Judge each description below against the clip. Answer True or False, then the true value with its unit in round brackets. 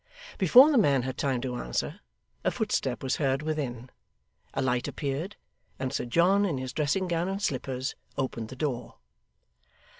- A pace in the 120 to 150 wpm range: False (160 wpm)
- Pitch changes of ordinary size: True (4.8 semitones)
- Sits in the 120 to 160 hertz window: True (135 Hz)